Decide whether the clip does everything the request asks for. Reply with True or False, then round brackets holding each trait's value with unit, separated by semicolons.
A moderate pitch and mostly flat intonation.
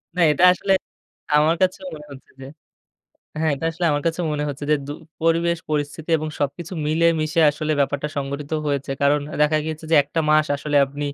True (155 Hz; 2.3 semitones)